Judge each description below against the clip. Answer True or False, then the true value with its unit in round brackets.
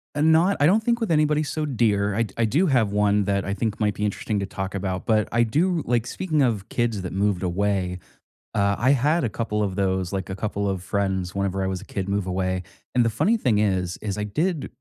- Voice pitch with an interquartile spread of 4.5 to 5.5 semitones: True (5.1 semitones)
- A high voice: False (105 Hz)